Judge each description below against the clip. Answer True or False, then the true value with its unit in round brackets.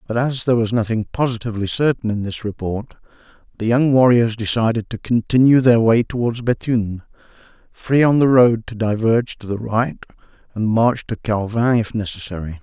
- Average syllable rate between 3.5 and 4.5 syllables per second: False (5.4 syllables/s)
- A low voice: True (115 Hz)